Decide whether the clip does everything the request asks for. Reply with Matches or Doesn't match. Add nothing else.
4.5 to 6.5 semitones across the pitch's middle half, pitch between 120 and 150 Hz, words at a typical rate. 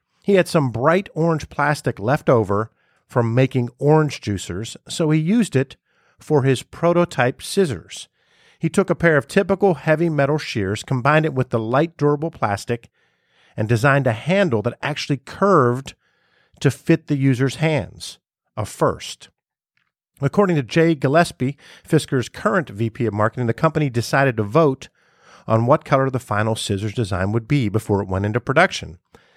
Matches